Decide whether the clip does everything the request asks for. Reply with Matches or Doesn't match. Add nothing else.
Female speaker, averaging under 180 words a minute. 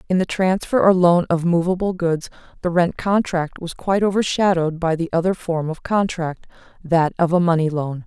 Doesn't match